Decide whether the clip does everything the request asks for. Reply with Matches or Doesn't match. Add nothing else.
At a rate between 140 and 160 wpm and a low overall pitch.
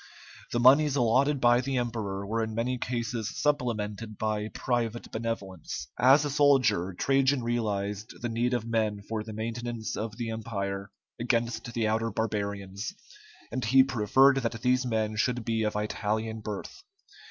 Matches